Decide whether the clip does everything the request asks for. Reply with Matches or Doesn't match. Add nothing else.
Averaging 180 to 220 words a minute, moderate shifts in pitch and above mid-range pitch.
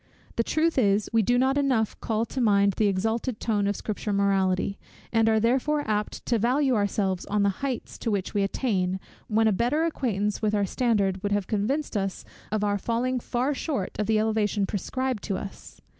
Matches